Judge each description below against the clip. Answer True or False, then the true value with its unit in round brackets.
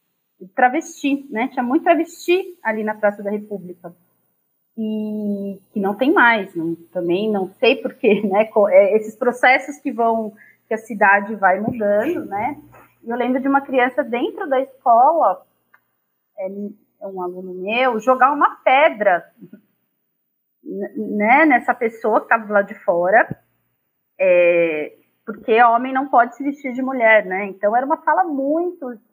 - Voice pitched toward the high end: True (230 Hz)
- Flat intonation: False (4.9 semitones)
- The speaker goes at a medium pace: True (140 wpm)